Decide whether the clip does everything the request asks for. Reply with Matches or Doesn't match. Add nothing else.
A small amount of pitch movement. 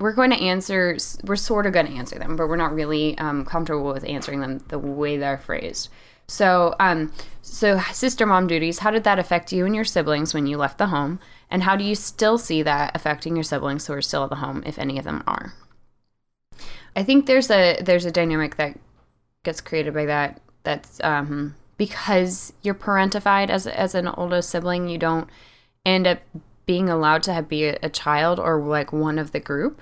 Doesn't match